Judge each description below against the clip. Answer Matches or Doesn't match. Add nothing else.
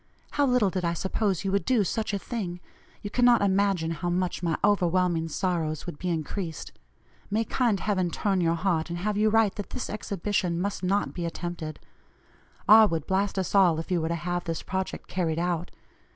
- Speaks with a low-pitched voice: Doesn't match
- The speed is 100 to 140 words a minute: Doesn't match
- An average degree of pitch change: Matches